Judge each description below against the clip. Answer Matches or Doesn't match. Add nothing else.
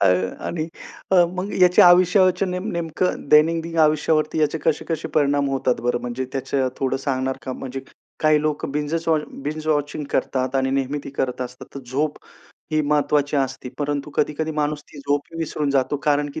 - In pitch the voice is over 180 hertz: Doesn't match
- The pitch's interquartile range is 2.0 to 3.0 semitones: Matches